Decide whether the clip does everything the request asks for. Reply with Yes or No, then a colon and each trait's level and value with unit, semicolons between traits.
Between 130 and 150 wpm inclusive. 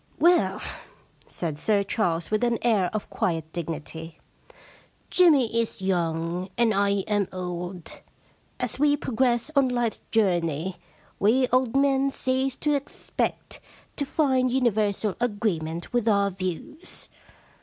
Yes: slow, 135 wpm